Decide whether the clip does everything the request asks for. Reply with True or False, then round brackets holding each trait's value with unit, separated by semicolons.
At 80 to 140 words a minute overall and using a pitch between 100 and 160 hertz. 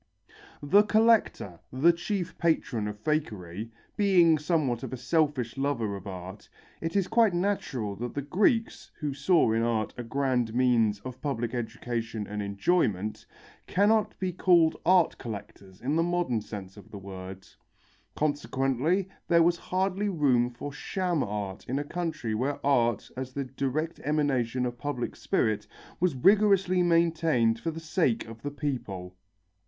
False (150 wpm; 135 Hz)